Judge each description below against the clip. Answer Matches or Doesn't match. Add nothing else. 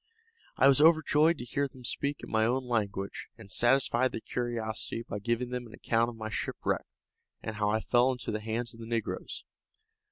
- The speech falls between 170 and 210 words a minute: Matches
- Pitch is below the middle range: Matches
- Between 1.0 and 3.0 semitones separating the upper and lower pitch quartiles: Matches